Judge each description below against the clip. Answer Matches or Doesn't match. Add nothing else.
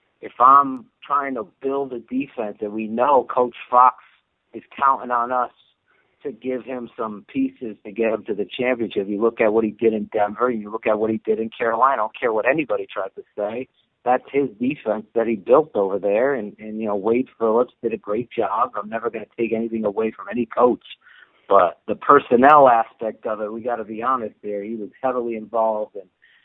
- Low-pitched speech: Matches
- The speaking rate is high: Matches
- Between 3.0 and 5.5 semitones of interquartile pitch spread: Doesn't match